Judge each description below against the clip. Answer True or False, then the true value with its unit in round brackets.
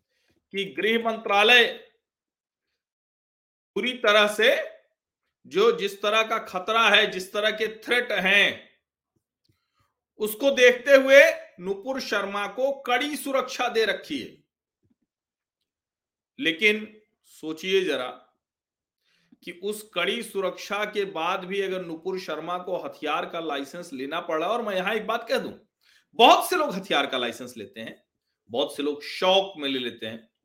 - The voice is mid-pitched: False (210 Hz)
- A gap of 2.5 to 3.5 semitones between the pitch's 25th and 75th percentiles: False (4.9 semitones)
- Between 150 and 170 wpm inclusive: False (135 wpm)